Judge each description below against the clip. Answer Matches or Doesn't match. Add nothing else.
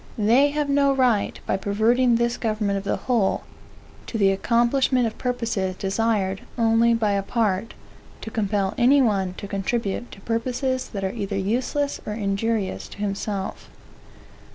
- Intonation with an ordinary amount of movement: Matches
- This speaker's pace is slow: Doesn't match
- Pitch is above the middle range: Matches